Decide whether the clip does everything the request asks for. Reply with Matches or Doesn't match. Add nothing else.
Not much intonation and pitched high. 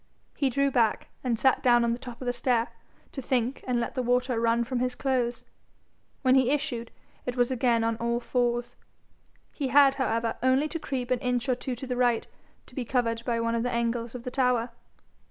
Matches